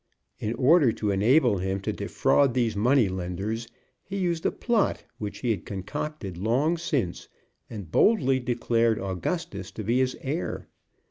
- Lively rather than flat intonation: Yes, wide, 6.0 semitones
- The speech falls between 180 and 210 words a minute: No, average, 150 wpm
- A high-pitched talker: No, low, 115 Hz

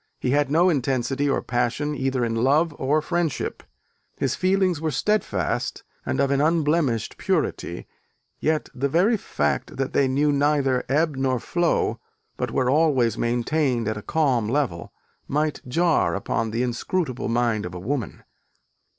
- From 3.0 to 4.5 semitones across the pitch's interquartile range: Yes, average, 4.2 semitones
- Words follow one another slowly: No, average, 150 wpm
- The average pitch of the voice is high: No, low, 135 Hz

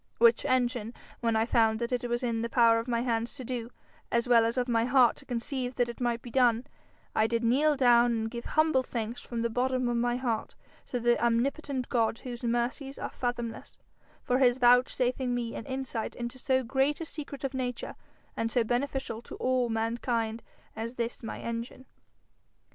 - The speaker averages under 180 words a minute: No, average, 195 wpm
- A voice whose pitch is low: No, high, 240 Hz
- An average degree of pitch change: No, narrow, 1.7 semitones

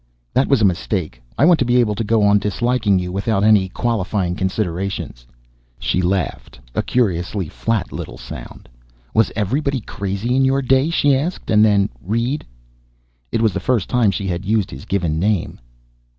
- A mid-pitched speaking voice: No, low, 105 Hz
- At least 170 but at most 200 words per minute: Yes, average, 180 wpm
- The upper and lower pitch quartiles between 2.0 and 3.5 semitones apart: No, average, 4.6 semitones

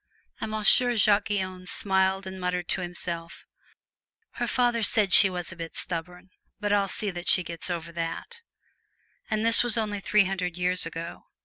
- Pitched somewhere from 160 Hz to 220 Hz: Yes, high, 190 Hz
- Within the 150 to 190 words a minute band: Yes, average, 175 wpm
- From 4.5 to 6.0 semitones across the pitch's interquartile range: No, average, 2.9 semitones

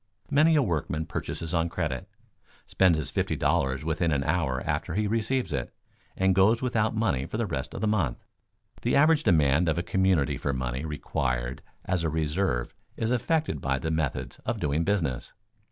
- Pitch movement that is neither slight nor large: No, wide, 6.7 semitones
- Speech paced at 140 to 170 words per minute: No, average, 180 wpm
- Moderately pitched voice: No, very low, 80 Hz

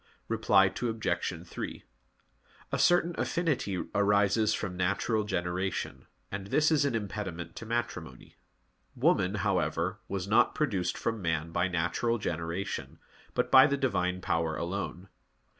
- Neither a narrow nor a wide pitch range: Yes, average, 4.3 semitones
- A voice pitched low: Yes, low, 100 Hz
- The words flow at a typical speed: No, slow, 125 wpm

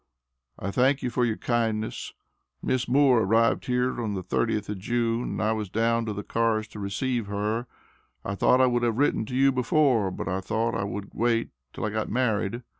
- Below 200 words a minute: No, fast, 205 wpm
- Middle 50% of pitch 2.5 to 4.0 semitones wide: Yes, average, 2.8 semitones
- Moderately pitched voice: No, low, 115 Hz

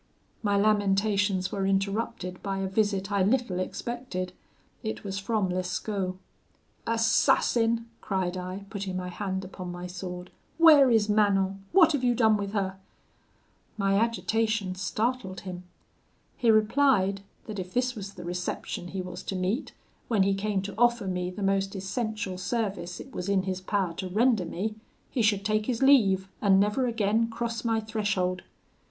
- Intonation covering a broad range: No, average, 3.0 semitones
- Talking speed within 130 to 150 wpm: No, average, 160 wpm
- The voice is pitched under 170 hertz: No, high, 200 Hz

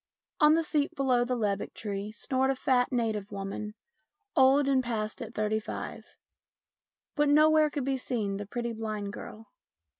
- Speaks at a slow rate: No, average, 160 wpm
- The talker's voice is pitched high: Yes, high, 240 Hz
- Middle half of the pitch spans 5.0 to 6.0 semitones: No, average, 4.3 semitones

